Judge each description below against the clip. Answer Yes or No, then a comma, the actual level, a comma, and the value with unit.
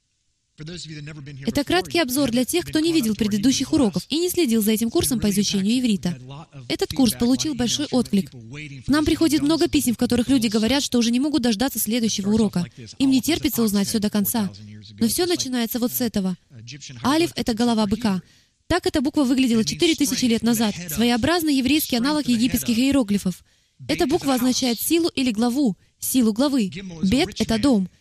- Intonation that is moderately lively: No, wide, 5.7 semitones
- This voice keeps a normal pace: No, fast, 170 wpm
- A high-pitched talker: Yes, high, 240 Hz